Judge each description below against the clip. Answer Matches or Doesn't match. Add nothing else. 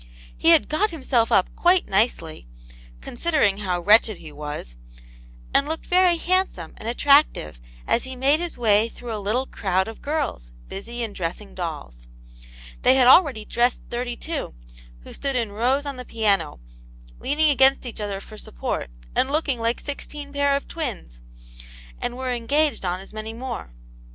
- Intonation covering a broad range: Matches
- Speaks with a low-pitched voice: Doesn't match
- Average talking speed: Matches